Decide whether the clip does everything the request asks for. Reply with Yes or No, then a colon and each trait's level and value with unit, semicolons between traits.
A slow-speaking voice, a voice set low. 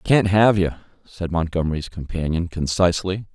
Yes: slow, 125 wpm; very low, 90 Hz